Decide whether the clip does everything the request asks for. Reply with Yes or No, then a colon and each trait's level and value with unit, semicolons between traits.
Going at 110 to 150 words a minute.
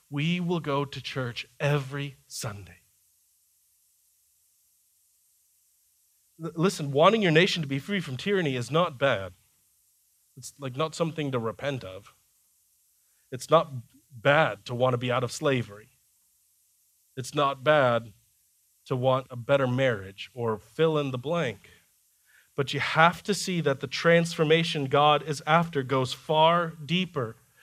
Yes: slow, 135 wpm